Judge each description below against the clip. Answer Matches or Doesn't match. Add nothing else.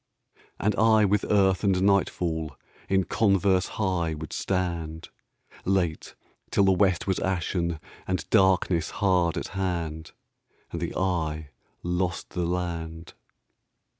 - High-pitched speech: Doesn't match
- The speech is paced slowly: Matches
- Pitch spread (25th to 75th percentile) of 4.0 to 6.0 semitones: Doesn't match